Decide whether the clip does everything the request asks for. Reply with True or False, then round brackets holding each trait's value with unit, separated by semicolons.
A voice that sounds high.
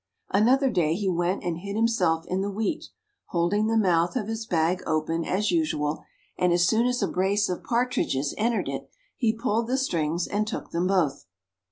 True (195 Hz)